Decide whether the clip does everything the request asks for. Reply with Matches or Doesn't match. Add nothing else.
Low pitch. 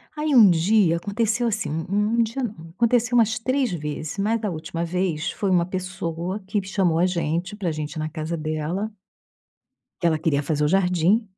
Doesn't match